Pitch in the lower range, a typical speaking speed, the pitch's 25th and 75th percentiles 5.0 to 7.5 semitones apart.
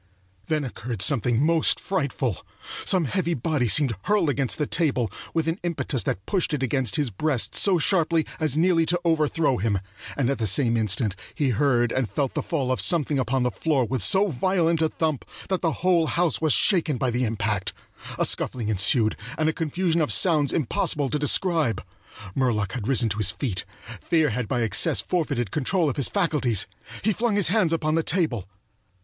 No: medium, 145 Hz; average, 190 wpm; wide, 5.4 semitones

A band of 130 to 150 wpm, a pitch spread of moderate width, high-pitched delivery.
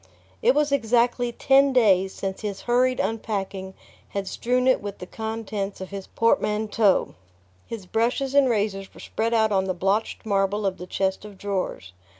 No: average, 165 wpm; average, 3.4 semitones; high, 210 Hz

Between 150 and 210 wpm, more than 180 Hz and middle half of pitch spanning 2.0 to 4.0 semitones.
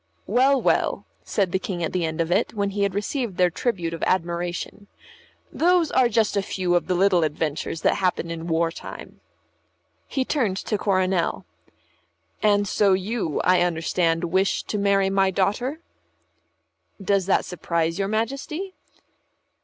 Yes: average, 155 wpm; high, 190 Hz; average, 3.2 semitones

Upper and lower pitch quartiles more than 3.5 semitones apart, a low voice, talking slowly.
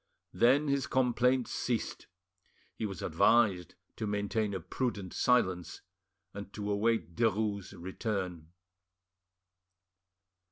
Yes: average, 4.0 semitones; low, 105 Hz; slow, 95 wpm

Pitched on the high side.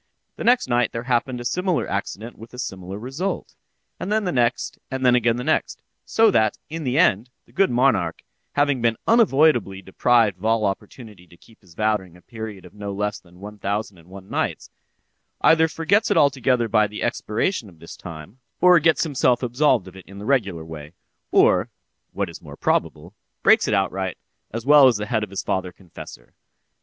No: low, 115 Hz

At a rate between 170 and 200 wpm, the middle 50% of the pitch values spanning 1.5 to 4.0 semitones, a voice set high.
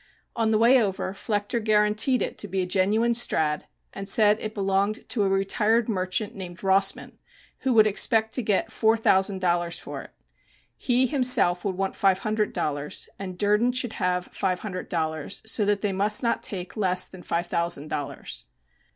Yes: average, 180 wpm; average, 3.1 semitones; high, 200 Hz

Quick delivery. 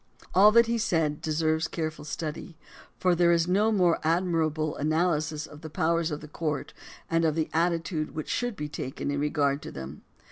No: average, 185 wpm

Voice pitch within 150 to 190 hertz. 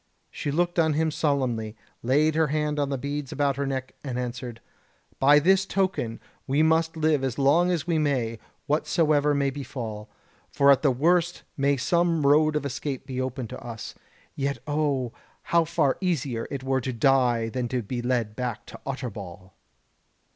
No: medium, 140 Hz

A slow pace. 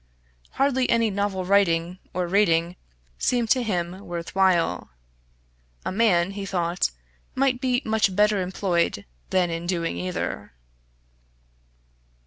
Yes: slow, 115 wpm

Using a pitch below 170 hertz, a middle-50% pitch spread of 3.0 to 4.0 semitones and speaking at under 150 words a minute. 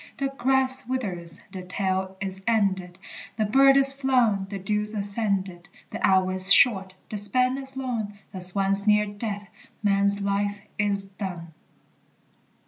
No: high, 200 Hz; average, 3.5 semitones; average, 140 wpm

